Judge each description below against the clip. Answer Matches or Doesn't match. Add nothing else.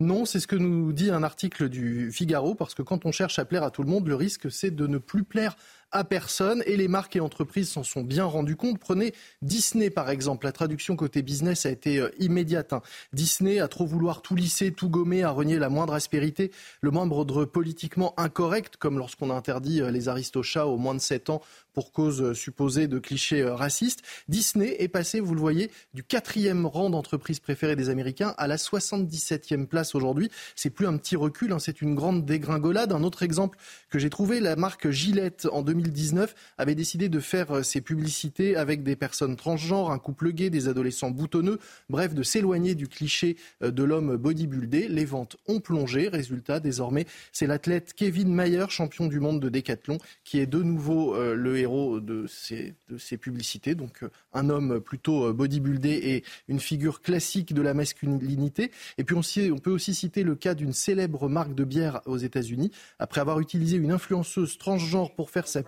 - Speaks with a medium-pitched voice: Matches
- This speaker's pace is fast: Doesn't match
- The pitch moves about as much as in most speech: Matches